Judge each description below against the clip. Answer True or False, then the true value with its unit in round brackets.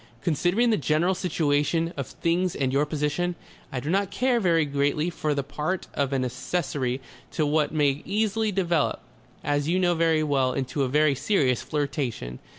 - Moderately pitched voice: True (150 Hz)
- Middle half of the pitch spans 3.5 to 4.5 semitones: True (4.0 semitones)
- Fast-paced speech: False (170 wpm)